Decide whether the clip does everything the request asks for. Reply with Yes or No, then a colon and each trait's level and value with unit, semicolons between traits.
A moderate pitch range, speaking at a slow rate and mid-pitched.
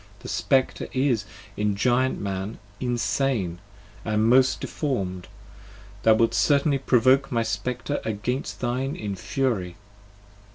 No: average, 4.0 semitones; slow, 120 wpm; low, 120 Hz